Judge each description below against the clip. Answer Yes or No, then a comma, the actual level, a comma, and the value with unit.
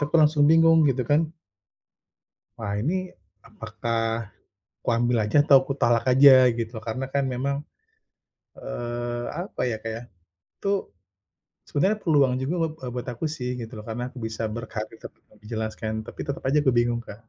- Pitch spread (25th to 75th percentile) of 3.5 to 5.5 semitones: Yes, average, 3.9 semitones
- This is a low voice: Yes, low, 125 Hz